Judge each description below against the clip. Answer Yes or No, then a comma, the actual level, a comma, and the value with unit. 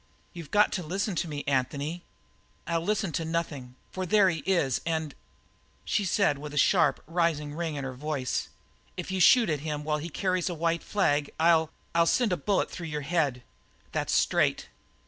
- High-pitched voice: No, medium, 165 Hz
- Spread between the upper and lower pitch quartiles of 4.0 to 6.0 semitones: No, average, 3.5 semitones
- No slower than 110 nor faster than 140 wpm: No, average, 195 wpm